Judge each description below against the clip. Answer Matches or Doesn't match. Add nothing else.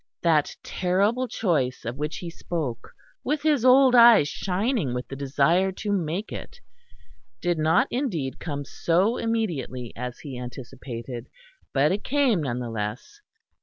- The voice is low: Doesn't match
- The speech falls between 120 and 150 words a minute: Matches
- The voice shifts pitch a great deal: Matches